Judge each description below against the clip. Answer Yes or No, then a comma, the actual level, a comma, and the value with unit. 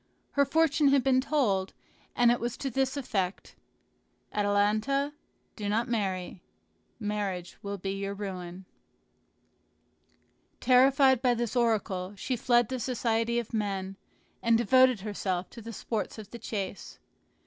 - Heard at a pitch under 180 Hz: No, high, 225 Hz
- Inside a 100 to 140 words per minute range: Yes, slow, 135 wpm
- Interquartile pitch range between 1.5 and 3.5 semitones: No, average, 4.3 semitones